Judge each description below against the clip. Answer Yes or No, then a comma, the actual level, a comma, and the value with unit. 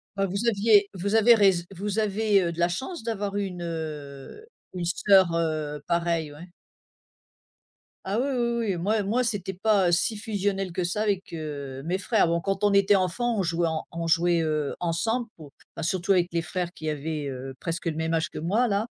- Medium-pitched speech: Yes, medium, 180 Hz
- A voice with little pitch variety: No, average, 3.8 semitones